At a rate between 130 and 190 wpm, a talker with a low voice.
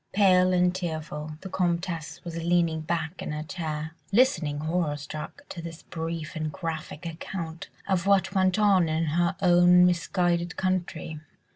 No: average, 150 wpm; medium, 170 Hz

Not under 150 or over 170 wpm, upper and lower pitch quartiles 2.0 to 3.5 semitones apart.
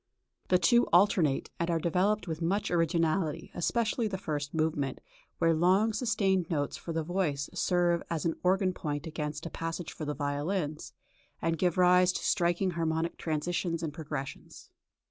Yes: average, 160 wpm; average, 2.7 semitones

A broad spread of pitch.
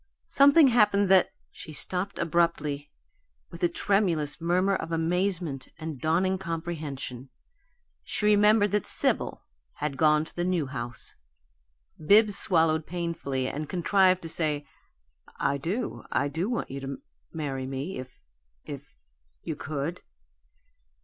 No: average, 4.6 semitones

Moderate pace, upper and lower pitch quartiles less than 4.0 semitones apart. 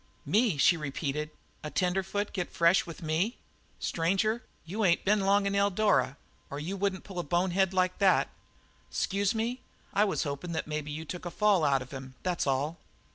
No: average, 185 wpm; average, 4.6 semitones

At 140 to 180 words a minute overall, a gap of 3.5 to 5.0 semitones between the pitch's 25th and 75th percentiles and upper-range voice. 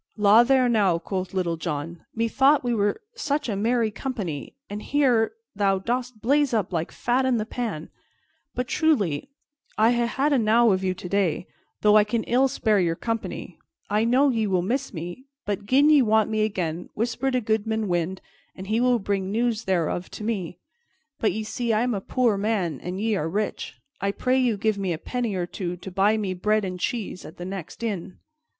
No: average, 200 wpm; average, 4.2 semitones; high, 215 Hz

